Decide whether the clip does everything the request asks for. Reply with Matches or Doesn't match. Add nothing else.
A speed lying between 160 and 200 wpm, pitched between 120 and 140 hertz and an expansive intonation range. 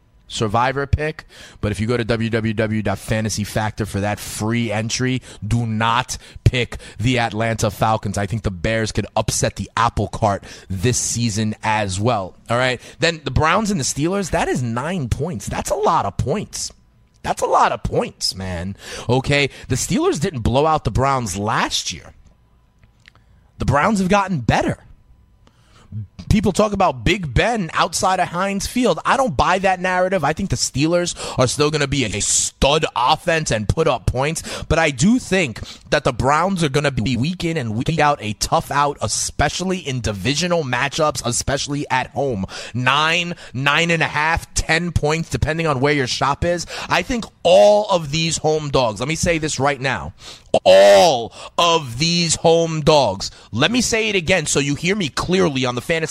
Matches